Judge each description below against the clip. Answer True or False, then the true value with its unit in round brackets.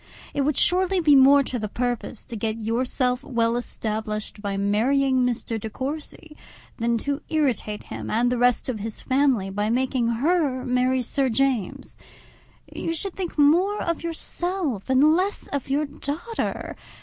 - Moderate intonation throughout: True (4.5 semitones)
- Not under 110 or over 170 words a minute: True (160 wpm)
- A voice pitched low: False (260 Hz)